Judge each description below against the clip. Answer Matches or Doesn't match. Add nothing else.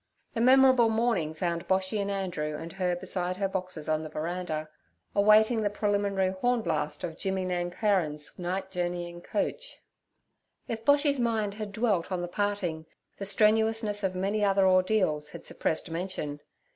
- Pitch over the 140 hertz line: Matches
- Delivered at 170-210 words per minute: Doesn't match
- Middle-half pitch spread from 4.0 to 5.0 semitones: Doesn't match